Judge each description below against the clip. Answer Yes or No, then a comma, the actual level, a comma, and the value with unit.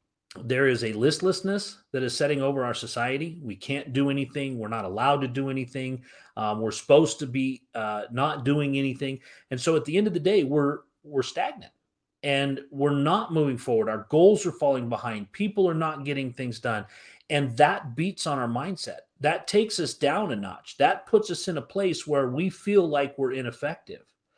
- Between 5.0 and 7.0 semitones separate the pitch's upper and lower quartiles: No, average, 3.9 semitones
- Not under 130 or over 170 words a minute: No, average, 195 wpm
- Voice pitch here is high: No, medium, 140 Hz